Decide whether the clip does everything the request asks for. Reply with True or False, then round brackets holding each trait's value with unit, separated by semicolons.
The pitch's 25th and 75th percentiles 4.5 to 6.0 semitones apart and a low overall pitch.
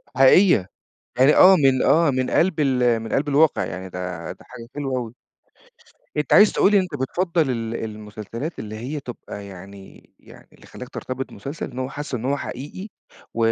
True (4.9 semitones; 130 Hz)